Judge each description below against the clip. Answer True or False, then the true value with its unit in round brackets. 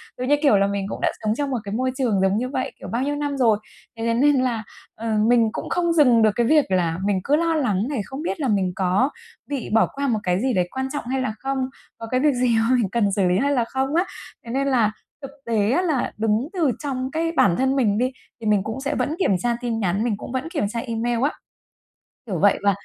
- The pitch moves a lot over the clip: False (4.3 semitones)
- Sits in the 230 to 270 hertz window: True (240 Hz)